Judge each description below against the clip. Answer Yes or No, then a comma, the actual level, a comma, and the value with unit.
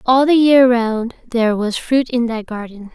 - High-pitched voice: Yes, high, 240 Hz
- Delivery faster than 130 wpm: Yes, fast, 205 wpm